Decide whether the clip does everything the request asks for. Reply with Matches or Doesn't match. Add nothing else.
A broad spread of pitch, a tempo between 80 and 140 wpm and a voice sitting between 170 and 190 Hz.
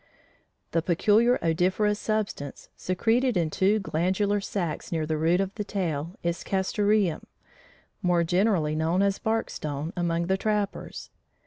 Doesn't match